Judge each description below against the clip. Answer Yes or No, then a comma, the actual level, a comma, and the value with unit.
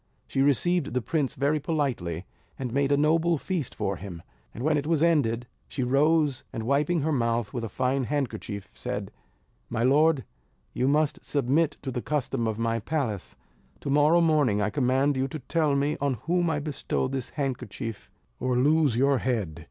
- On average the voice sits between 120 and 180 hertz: Yes, low, 135 Hz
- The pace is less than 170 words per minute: No, average, 180 wpm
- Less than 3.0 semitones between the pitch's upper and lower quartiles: No, average, 4.1 semitones